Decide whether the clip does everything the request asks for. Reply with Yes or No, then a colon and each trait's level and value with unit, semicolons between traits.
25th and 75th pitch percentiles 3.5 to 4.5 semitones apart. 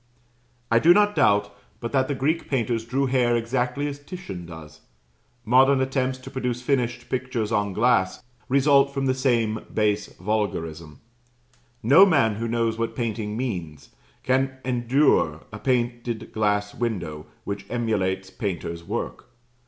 Yes: average, 4.2 semitones